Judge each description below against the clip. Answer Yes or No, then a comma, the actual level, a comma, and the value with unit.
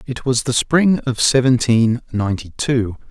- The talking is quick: No, average, 155 wpm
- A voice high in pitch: No, low, 125 Hz